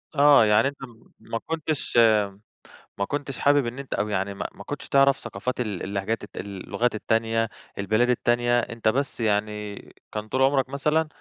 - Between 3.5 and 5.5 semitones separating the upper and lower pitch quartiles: Yes, average, 4.5 semitones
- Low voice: Yes, low, 120 Hz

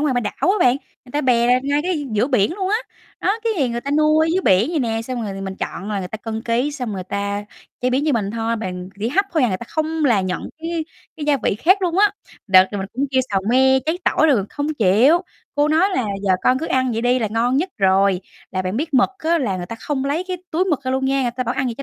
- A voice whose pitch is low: No, very high, 255 Hz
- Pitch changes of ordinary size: No, wide, 6.1 semitones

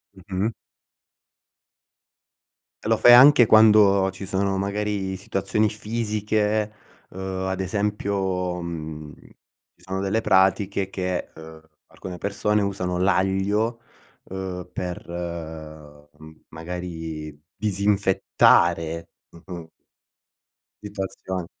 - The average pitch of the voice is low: Yes, very low, 95 Hz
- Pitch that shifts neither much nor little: Yes, average, 3.0 semitones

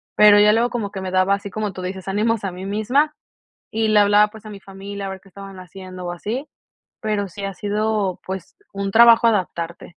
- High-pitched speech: Yes, high, 200 Hz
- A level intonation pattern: Yes, narrow, 2.1 semitones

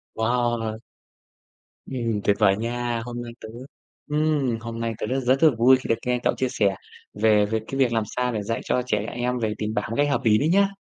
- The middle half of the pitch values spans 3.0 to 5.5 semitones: No, narrow, 2.4 semitones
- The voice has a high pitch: No, low, 120 Hz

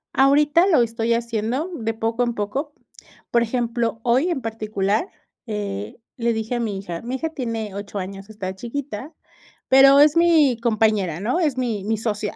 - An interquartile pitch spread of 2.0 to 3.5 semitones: No, average, 4.1 semitones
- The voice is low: No, high, 230 Hz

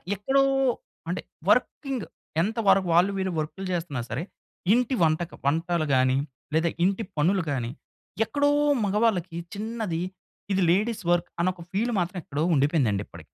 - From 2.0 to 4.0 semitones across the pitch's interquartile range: No, average, 5.0 semitones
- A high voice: No, medium, 180 Hz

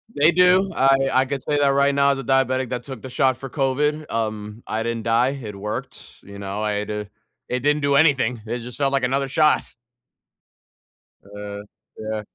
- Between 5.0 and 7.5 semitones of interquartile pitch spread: No, average, 4.3 semitones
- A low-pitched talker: Yes, low, 130 Hz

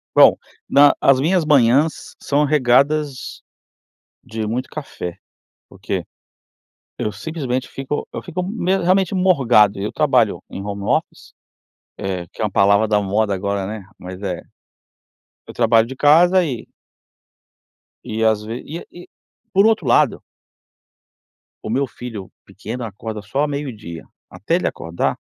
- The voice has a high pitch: No, low, 120 Hz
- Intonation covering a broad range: Yes, wide, 6.2 semitones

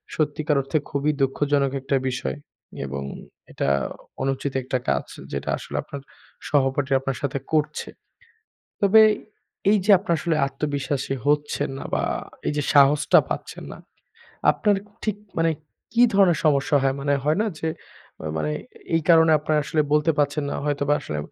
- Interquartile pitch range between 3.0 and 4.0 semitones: No, narrow, 2.4 semitones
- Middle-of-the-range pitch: Yes, medium, 145 Hz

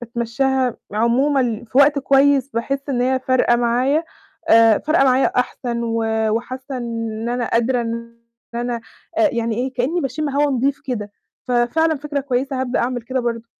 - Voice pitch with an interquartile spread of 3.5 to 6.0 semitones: No, narrow, 2.6 semitones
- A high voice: Yes, very high, 250 Hz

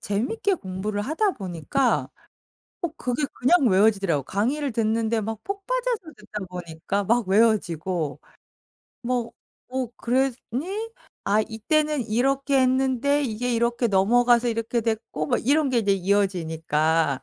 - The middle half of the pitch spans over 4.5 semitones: Yes, average, 5.2 semitones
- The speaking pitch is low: No, high, 230 Hz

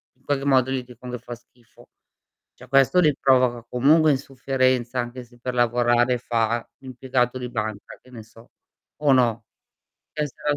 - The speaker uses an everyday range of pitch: No, narrow, 1.9 semitones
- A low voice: Yes, low, 125 Hz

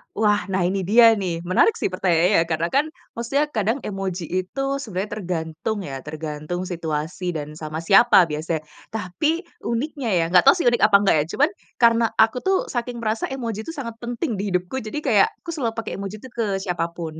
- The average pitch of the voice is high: Yes, high, 200 Hz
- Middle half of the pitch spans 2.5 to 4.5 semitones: No, average, 5.3 semitones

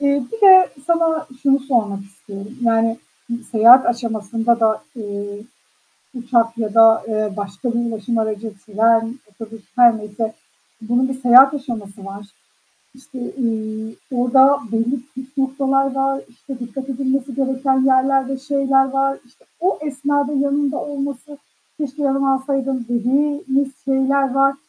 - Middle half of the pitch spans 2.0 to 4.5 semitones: Yes, average, 3.4 semitones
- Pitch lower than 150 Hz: No, very high, 260 Hz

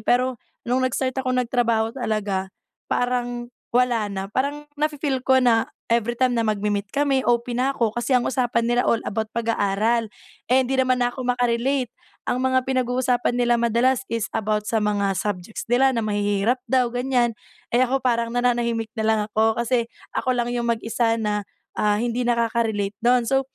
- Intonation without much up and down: Yes, narrow, 2.3 semitones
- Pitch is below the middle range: No, high, 240 Hz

